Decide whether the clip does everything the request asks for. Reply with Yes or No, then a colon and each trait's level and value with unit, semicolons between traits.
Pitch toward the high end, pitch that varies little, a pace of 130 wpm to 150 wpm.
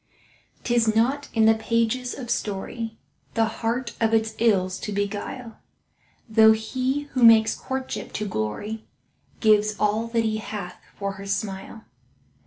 Yes: high, 220 Hz; narrow, 1.8 semitones; average, 140 wpm